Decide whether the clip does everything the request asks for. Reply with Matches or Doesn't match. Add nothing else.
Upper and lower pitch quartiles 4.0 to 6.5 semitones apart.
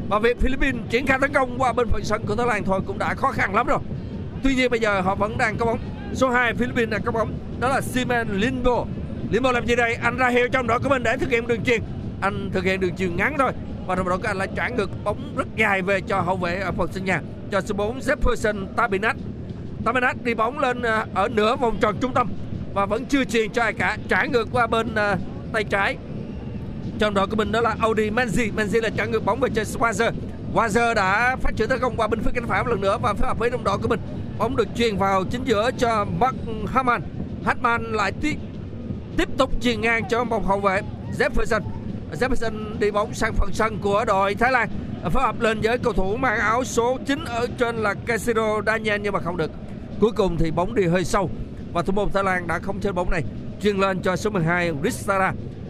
Doesn't match